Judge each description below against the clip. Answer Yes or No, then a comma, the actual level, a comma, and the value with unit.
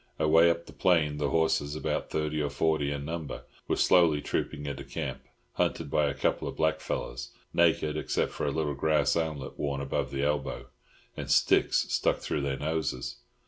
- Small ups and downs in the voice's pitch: Yes, narrow, 2.0 semitones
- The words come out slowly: No, average, 175 wpm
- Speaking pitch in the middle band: No, very low, 75 Hz